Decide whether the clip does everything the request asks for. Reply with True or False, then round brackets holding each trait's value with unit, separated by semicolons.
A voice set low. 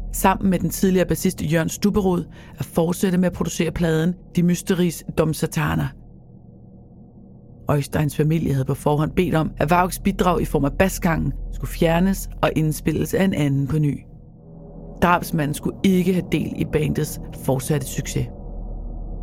False (165 Hz)